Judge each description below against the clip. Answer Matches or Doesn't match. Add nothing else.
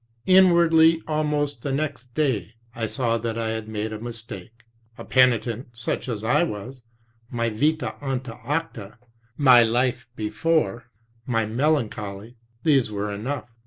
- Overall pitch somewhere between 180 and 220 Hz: Doesn't match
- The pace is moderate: Doesn't match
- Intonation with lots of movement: Doesn't match